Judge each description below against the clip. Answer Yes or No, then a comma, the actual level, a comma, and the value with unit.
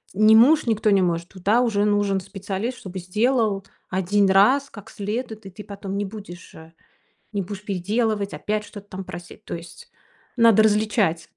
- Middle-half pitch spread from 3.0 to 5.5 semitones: No, narrow, 2.4 semitones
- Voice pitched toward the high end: Yes, high, 205 Hz